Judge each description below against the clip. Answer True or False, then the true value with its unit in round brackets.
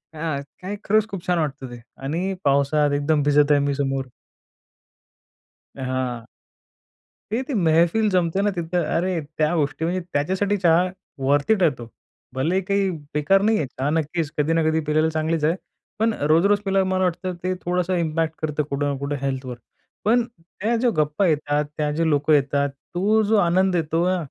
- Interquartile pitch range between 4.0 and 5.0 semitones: True (4.3 semitones)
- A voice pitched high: False (160 Hz)